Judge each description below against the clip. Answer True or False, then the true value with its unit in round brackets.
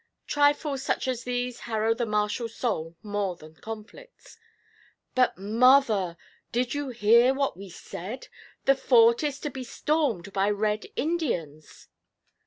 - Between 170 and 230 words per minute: False (135 wpm)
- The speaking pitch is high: True (235 Hz)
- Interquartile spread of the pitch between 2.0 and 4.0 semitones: False (4.4 semitones)